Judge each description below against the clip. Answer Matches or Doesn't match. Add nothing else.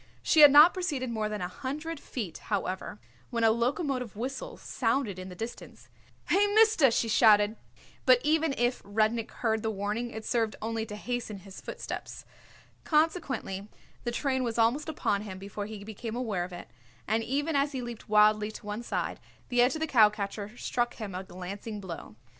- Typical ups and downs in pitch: Matches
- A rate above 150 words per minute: Matches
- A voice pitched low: Doesn't match